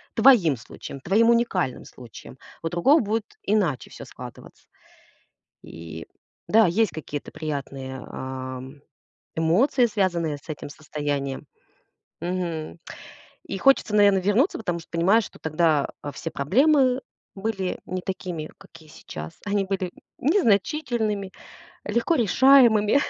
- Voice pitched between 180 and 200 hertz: Yes, medium, 185 Hz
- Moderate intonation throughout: No, wide, 6.8 semitones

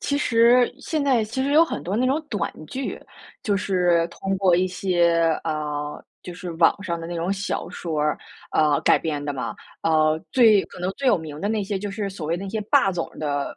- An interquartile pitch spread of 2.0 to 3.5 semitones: No, average, 4.7 semitones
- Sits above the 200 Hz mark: No, medium, 185 Hz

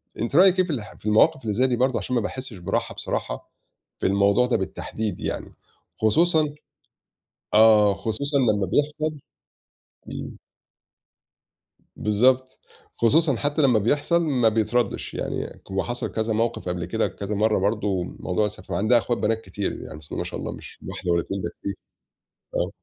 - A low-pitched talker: Yes, low, 110 Hz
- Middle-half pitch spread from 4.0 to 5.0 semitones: Yes, average, 4.4 semitones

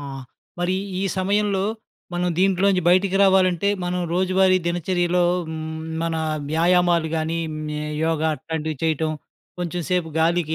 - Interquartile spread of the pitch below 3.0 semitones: Yes, narrow, 2.4 semitones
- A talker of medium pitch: Yes, medium, 175 Hz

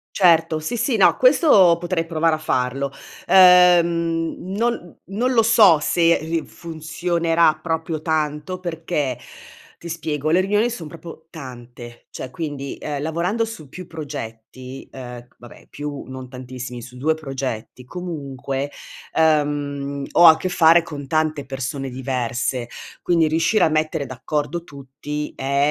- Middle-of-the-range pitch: Yes, medium, 155 Hz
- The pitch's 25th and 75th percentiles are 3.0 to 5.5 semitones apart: Yes, average, 3.8 semitones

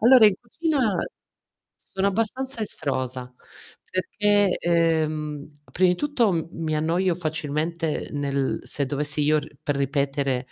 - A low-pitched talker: No, medium, 160 Hz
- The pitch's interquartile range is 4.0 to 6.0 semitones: Yes, wide, 5.6 semitones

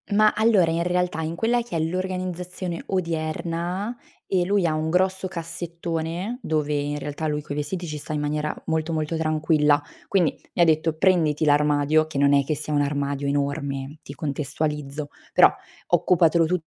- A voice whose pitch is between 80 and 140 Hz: No, medium, 160 Hz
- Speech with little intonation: No, average, 3.1 semitones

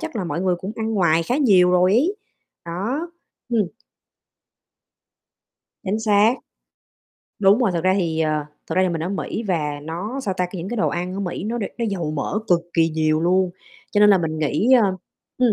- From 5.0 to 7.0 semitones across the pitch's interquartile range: No, average, 4.3 semitones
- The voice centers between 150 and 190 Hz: Yes, medium, 185 Hz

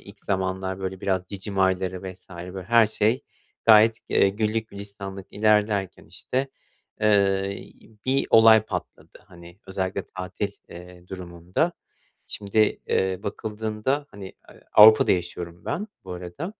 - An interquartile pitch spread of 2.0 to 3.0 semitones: Yes, narrow, 2.5 semitones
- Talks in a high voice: No, low, 100 Hz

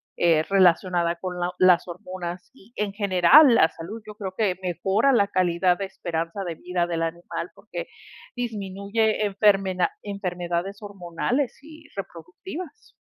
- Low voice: No, medium, 185 Hz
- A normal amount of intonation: Yes, average, 3.2 semitones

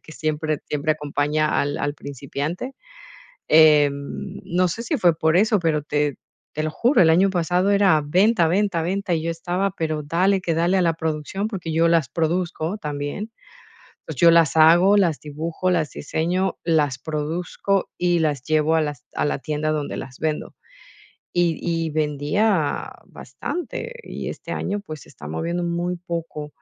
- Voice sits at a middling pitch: Yes, medium, 165 Hz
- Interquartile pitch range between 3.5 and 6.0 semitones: No, average, 3.0 semitones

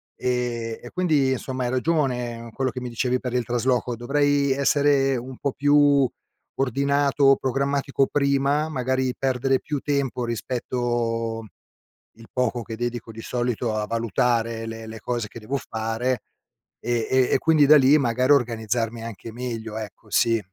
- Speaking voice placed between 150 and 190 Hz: No, low, 125 Hz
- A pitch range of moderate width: Yes, average, 3.0 semitones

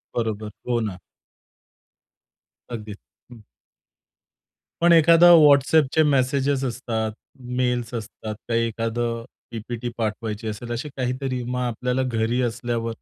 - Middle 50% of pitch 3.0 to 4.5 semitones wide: No, narrow, 2.4 semitones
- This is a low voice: Yes, low, 120 Hz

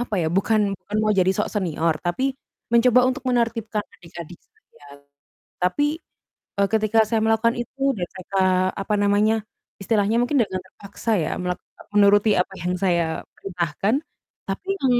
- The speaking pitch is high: Yes, high, 205 Hz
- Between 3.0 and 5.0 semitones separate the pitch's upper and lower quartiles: Yes, average, 3.8 semitones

